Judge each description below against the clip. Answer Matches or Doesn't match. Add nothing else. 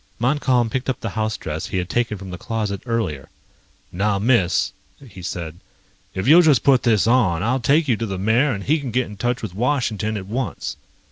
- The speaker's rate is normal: Doesn't match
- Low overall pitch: Matches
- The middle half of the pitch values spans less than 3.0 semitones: Doesn't match